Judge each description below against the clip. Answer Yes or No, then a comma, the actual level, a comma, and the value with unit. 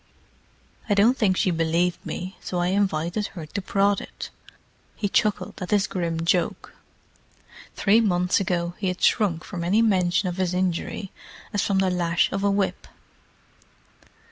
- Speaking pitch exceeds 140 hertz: Yes, medium, 185 Hz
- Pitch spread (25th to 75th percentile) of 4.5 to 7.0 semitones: No, narrow, 2.4 semitones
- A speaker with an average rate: Yes, average, 160 wpm